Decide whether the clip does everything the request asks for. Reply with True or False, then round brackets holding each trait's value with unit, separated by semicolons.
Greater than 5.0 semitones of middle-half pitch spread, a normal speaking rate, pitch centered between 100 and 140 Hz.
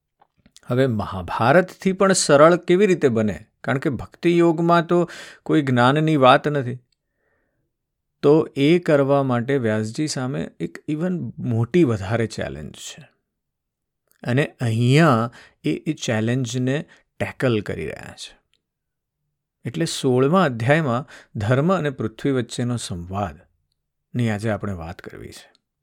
True (5.4 semitones; 115 wpm; 135 Hz)